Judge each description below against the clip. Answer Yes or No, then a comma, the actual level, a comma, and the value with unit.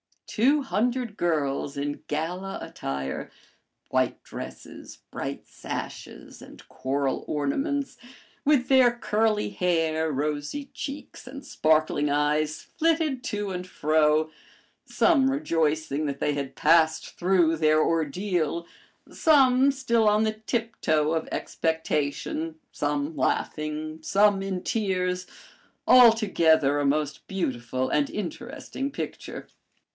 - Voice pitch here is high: No, medium, 165 Hz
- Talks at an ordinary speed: No, slow, 110 wpm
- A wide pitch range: Yes, wide, 7.0 semitones